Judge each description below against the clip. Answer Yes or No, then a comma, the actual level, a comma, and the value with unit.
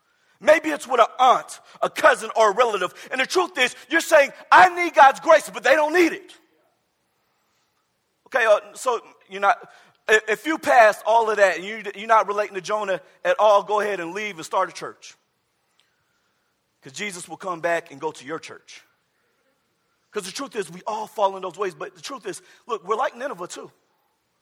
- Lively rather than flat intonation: Yes, wide, 7.2 semitones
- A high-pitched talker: Yes, high, 215 Hz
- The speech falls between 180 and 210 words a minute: Yes, average, 195 wpm